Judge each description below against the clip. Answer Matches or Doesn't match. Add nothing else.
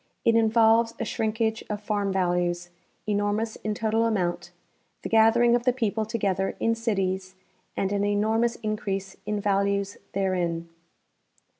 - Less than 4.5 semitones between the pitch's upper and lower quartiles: Matches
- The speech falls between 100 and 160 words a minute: Matches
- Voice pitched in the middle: Doesn't match